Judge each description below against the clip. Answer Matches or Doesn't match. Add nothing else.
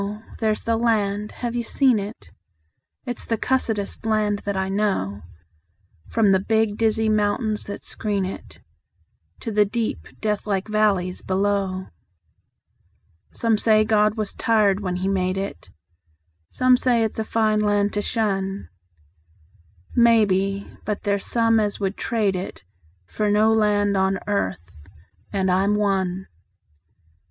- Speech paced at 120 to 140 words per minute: Matches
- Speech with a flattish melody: Matches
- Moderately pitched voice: Doesn't match